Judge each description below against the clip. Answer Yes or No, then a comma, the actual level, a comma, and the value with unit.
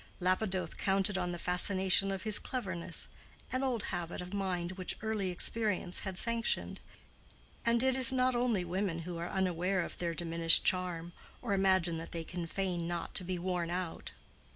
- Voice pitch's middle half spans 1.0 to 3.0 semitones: Yes, narrow, 2.6 semitones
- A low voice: No, medium, 185 Hz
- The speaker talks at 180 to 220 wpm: No, average, 170 wpm